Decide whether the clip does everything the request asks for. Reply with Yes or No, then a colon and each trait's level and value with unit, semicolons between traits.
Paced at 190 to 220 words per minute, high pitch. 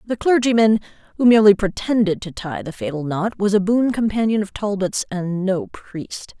No: average, 180 wpm; high, 205 Hz